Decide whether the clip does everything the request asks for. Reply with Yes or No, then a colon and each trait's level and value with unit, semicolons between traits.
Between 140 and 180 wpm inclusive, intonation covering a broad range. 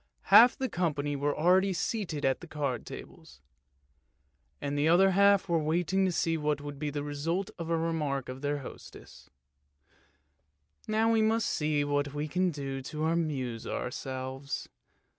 No: average, 165 wpm; average, 4.2 semitones